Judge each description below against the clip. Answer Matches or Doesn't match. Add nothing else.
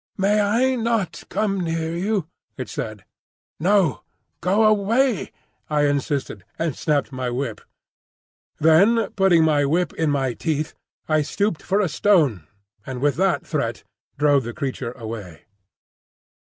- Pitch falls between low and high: Matches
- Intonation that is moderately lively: Doesn't match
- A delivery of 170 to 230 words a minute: Doesn't match